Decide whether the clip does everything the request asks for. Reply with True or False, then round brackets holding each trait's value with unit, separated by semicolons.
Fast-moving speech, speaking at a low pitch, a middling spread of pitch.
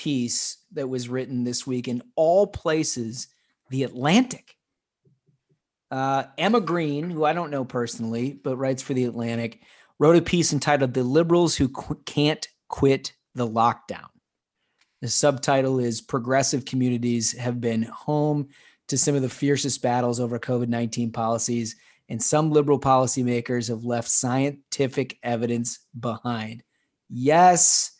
False (135 wpm; 130 Hz; 3.3 semitones)